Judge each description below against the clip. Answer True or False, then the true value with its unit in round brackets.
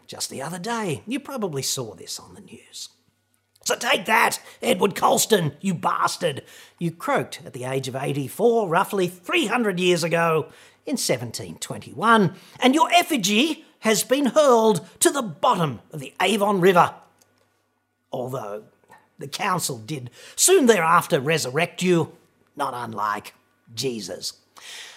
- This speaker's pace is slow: True (130 wpm)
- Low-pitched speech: False (185 Hz)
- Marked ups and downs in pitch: True (7.1 semitones)